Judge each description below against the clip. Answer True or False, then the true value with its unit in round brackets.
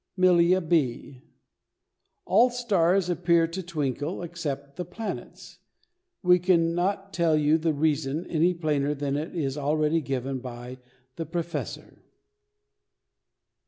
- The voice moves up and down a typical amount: True (3.6 semitones)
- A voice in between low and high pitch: True (165 Hz)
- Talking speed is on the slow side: True (115 wpm)